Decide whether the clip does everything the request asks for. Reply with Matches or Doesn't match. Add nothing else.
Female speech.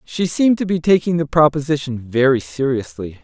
Doesn't match